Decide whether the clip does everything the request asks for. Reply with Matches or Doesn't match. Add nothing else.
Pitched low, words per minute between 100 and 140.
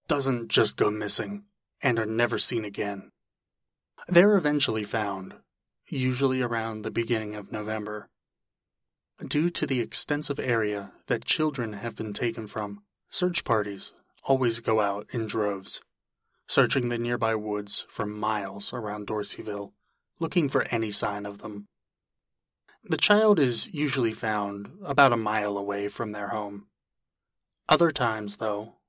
Matches